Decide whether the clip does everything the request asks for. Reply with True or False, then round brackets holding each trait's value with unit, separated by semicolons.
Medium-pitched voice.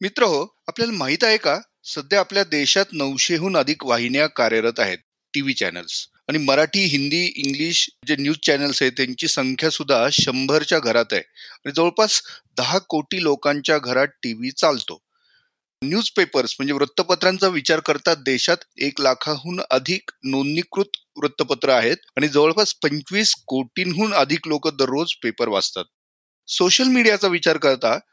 True (155 Hz)